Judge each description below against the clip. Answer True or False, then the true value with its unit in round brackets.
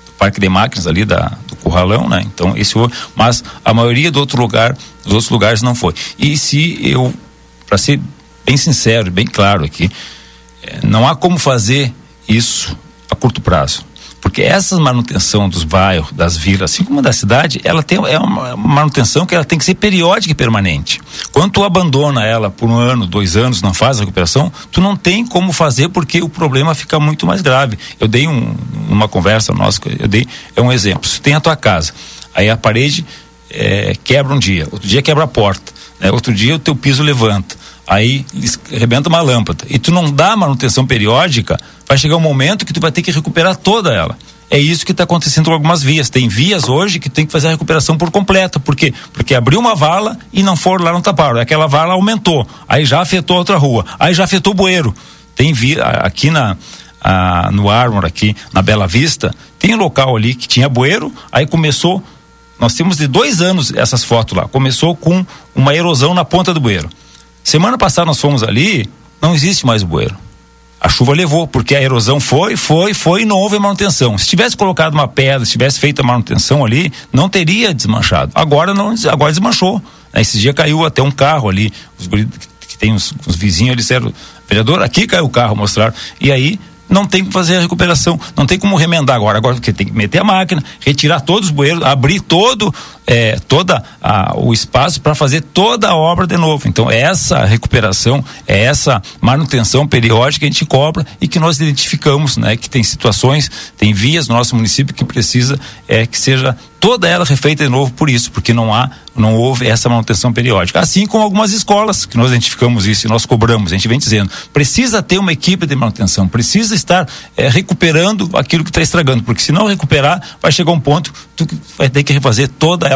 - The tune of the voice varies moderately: False (6.5 semitones)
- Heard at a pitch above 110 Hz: True (140 Hz)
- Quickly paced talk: True (205 wpm)